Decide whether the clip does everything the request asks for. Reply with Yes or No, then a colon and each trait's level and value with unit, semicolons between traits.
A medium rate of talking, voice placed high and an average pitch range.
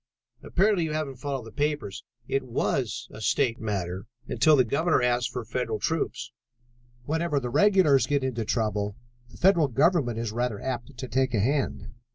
No: average, 170 wpm; low, 130 Hz; average, 4.4 semitones